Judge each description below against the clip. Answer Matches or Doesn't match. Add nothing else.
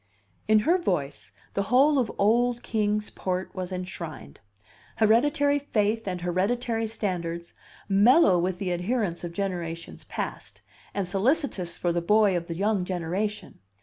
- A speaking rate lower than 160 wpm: Matches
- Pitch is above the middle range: Matches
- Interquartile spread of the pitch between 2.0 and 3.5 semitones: Doesn't match